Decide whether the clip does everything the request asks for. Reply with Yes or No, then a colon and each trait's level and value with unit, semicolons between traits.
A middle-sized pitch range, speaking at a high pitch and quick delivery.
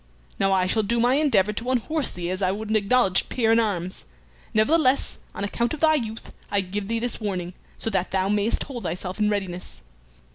Yes: average, 3.8 semitones; high, 210 Hz; fast, 210 wpm